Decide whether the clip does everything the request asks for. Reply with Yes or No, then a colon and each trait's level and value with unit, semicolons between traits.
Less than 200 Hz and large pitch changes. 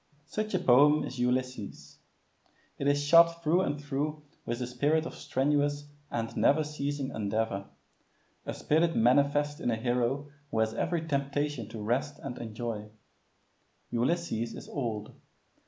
No: medium, 140 Hz; average, 3.8 semitones